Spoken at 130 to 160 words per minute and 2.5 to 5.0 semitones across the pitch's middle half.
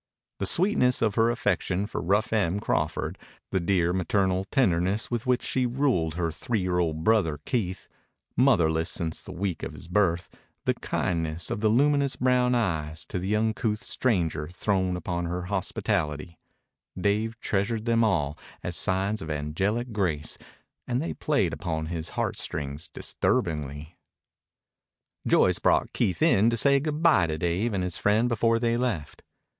No: average, 155 wpm; wide, 5.5 semitones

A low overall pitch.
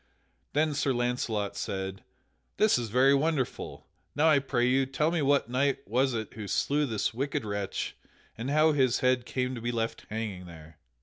Yes: low, 125 Hz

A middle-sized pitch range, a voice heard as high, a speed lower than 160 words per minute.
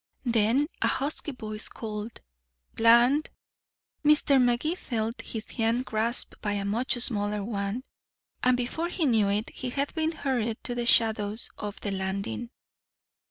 Yes: average, 3.2 semitones; high, 230 Hz; average, 145 wpm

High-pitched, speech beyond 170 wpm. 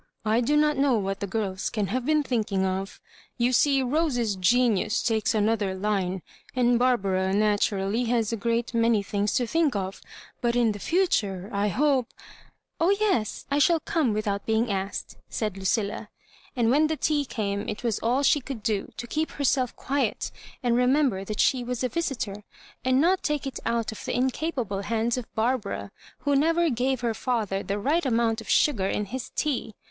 Yes: high, 235 Hz; average, 190 wpm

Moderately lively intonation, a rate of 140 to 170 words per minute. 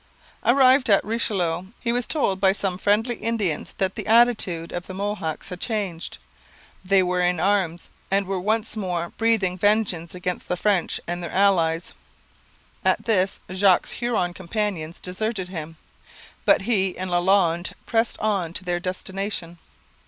Yes: average, 3.1 semitones; average, 150 wpm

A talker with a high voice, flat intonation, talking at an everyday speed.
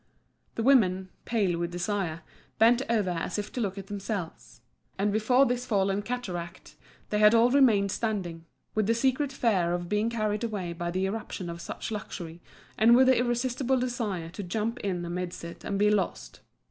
No: high, 205 Hz; average, 4.5 semitones; average, 175 wpm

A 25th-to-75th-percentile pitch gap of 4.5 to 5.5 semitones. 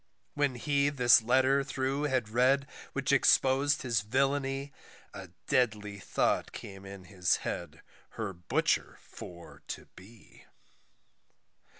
Yes: average, 5.0 semitones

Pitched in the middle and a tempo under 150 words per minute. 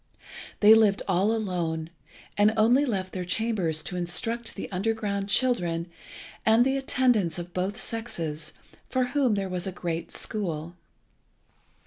No: high, 200 Hz; slow, 135 wpm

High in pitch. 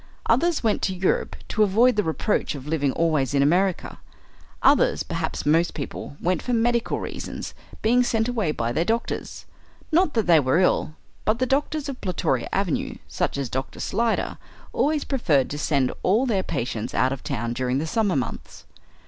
No: medium, 180 Hz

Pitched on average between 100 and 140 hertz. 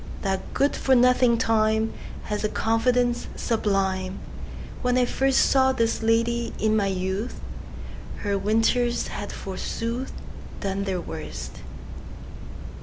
No: high, 225 Hz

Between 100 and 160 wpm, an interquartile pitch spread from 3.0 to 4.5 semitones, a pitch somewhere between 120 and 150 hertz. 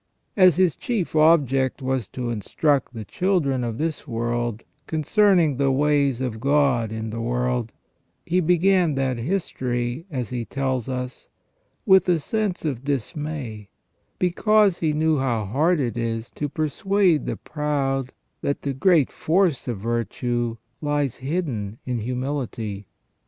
No: average, 140 wpm; average, 4.9 semitones; low, 135 Hz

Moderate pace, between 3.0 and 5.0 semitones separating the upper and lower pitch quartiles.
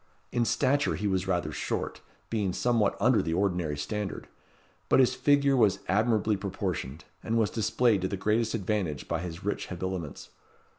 Yes: average, 160 wpm; average, 4.1 semitones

